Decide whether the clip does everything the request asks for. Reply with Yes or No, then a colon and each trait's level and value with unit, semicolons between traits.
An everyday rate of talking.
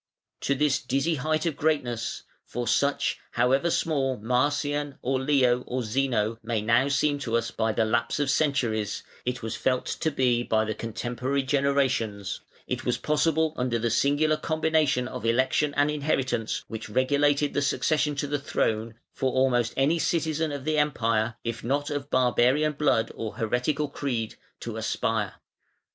Yes: average, 160 wpm